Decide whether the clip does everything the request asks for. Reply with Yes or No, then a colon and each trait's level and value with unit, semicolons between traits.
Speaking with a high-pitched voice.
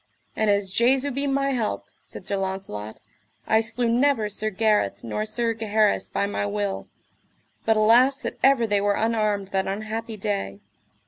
Yes: high, 215 Hz